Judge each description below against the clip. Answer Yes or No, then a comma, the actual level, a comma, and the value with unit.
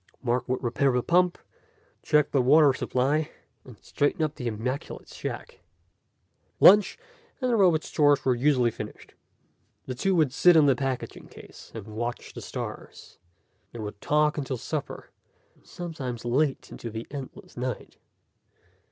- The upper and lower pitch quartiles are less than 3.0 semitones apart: No, average, 3.8 semitones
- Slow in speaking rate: No, average, 150 wpm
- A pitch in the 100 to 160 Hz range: Yes, low, 135 Hz